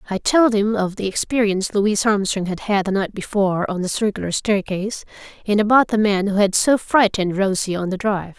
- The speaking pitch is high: Yes, high, 205 Hz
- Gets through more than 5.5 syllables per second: Yes, 5.8 syllables/s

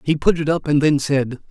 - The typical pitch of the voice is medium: Yes, medium, 150 Hz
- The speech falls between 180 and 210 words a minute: No, fast, 280 wpm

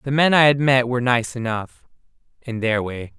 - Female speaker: No, male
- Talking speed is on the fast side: No, average, 190 wpm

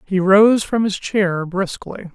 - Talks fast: No, average, 170 wpm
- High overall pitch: Yes, high, 195 Hz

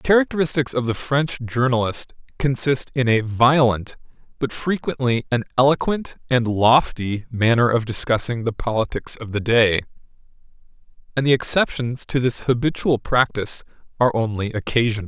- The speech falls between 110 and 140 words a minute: Yes, slow, 135 wpm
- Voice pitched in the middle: No, low, 125 Hz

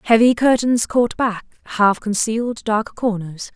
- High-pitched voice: Yes, high, 220 Hz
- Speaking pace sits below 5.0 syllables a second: Yes, 4.1 syllables/s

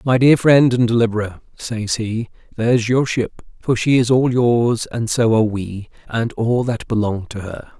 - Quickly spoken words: No, average, 195 wpm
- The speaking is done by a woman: No, male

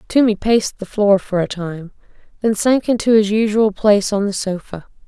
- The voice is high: Yes, high, 205 Hz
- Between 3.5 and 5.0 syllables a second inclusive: No, 5.2 syllables/s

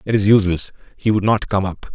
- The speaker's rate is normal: No, fast, 245 wpm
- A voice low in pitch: Yes, low, 100 Hz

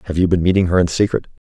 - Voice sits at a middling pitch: No, very low, 90 Hz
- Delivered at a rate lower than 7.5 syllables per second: No, 8.0 syllables/s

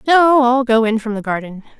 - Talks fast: Yes, fast, 235 wpm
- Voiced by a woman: Yes, female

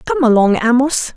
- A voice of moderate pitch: No, high, 245 Hz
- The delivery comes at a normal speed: Yes, average, 155 wpm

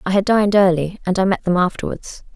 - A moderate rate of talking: No, fast, 230 wpm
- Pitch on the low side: No, high, 190 Hz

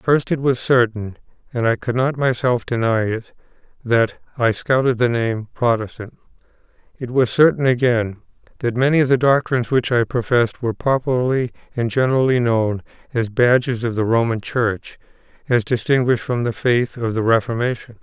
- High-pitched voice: No, low, 120 Hz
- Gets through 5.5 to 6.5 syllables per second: No, 5.1 syllables/s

